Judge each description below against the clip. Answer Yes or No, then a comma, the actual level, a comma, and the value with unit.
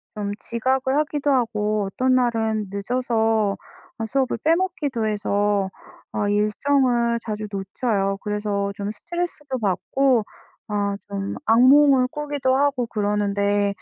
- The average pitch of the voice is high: Yes, high, 225 Hz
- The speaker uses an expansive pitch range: No, average, 4.4 semitones